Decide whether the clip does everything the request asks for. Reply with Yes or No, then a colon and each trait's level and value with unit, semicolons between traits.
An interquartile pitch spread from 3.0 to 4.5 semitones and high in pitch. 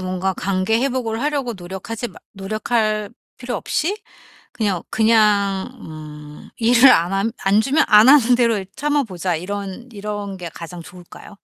Yes: average, 3.9 semitones; high, 205 Hz